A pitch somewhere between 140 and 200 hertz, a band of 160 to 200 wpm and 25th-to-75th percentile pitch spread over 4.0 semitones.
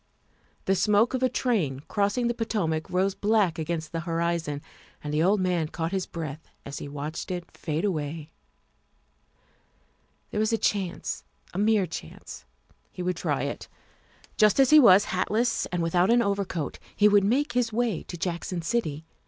Yes: medium, 185 Hz; average, 170 wpm; average, 4.6 semitones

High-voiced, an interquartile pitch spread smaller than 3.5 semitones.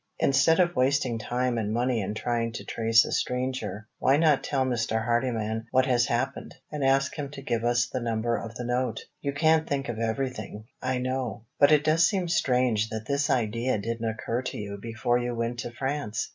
No: low, 120 Hz; average, 3.0 semitones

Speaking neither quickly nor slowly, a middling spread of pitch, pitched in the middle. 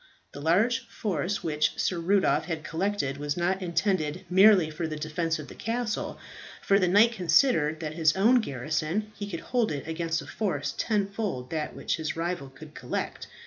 Yes: average, 185 wpm; average, 4.7 semitones; medium, 170 Hz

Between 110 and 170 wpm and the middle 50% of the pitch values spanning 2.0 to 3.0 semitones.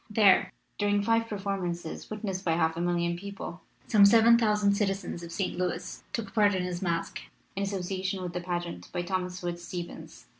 No: average, 185 wpm; average, 2.7 semitones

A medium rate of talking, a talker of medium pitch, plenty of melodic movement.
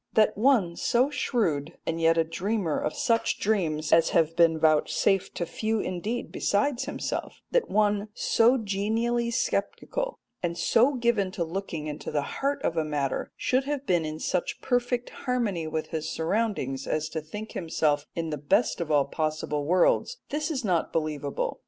Yes: average, 170 wpm; medium, 180 Hz; wide, 6.8 semitones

